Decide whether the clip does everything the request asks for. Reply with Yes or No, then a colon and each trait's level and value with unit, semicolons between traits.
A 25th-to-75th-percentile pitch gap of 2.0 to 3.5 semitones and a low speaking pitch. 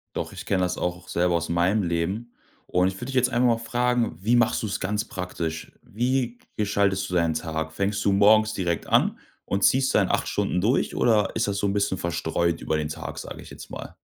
No: average, 4.7 semitones; low, 100 Hz